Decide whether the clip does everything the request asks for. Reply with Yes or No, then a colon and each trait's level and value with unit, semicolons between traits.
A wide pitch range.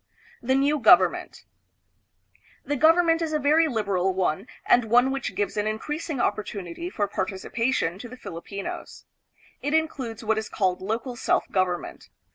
Yes: wide, 6.4 semitones